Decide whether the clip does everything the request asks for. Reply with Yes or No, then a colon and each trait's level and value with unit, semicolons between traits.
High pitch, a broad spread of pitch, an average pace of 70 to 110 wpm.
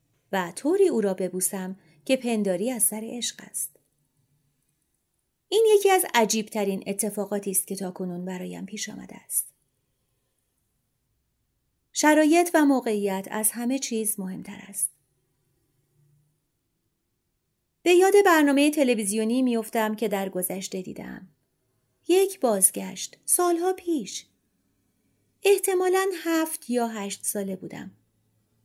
Yes: high, 210 Hz; wide, 7.1 semitones; slow, 105 wpm